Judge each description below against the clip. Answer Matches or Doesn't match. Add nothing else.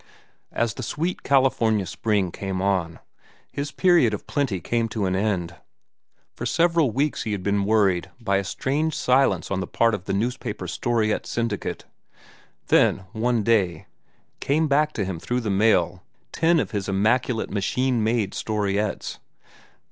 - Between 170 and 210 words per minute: Doesn't match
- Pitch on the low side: Matches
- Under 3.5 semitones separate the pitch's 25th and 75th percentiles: Doesn't match